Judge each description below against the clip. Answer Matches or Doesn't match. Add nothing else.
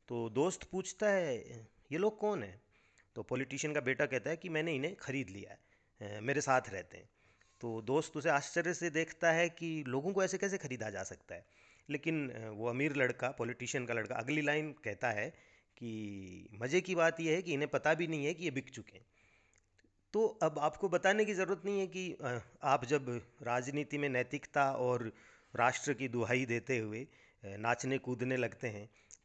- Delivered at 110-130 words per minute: Doesn't match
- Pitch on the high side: Doesn't match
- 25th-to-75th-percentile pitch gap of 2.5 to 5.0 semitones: Doesn't match